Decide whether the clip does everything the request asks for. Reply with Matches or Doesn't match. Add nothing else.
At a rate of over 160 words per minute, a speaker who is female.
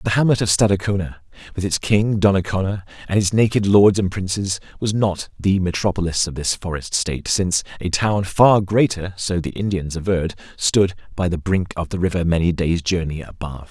Doesn't match